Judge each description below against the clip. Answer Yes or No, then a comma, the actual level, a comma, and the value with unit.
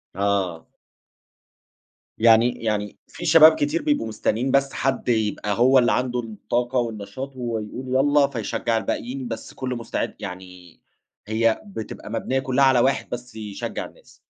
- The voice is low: Yes, low, 120 Hz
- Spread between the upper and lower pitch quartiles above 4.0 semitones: No, average, 3.5 semitones